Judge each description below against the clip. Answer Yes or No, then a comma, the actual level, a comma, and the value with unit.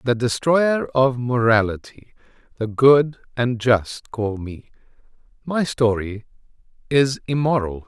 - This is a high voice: No, low, 120 Hz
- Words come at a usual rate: No, slow, 105 wpm